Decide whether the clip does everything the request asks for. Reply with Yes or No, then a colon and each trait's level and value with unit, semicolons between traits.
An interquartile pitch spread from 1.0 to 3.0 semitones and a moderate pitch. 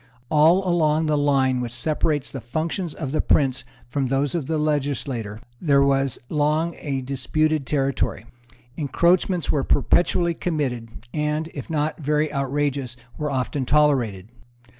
Yes: average, 2.7 semitones; medium, 145 Hz